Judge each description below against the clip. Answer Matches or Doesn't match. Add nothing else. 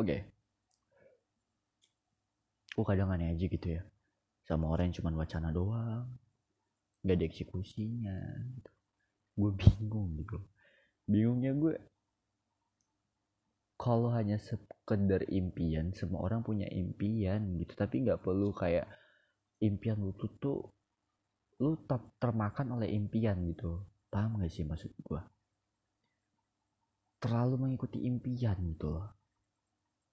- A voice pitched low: Matches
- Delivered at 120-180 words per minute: Doesn't match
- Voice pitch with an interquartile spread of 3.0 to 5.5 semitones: Doesn't match